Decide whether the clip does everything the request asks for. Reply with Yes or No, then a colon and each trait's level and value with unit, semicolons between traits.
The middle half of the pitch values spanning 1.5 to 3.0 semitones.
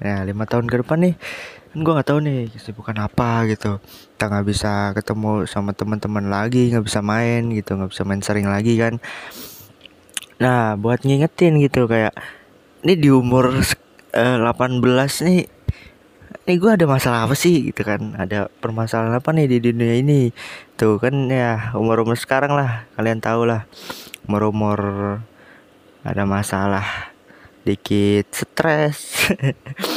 No: average, 4.3 semitones